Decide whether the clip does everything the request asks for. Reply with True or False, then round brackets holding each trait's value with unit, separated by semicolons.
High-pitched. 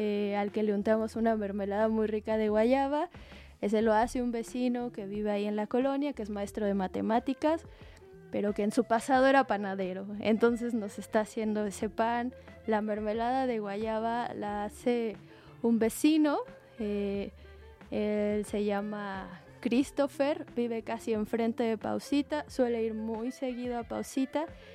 True (220 Hz)